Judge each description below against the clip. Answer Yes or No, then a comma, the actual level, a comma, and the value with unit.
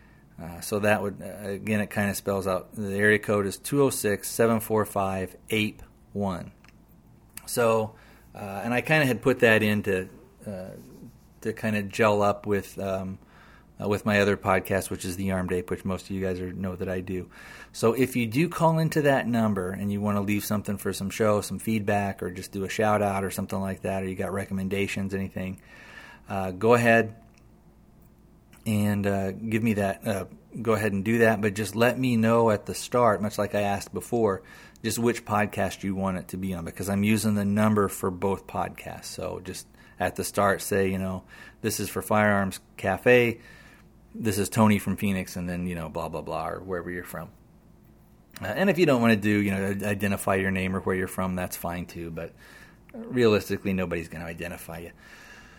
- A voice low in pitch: Yes, low, 100 Hz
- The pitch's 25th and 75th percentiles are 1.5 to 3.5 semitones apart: Yes, narrow, 2.4 semitones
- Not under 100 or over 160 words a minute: No, fast, 205 wpm